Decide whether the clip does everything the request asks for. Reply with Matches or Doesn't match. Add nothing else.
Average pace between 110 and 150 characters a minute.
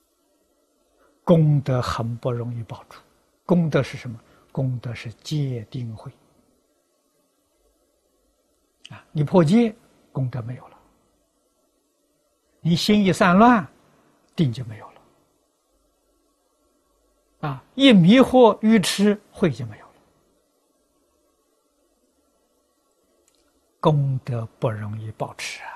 Matches